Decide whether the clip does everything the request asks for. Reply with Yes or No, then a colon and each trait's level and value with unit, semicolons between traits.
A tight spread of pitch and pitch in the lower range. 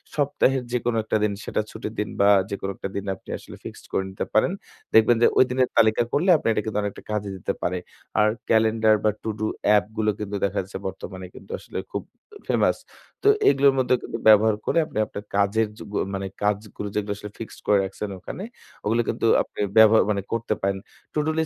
Yes: narrow, 2.2 semitones; low, 110 Hz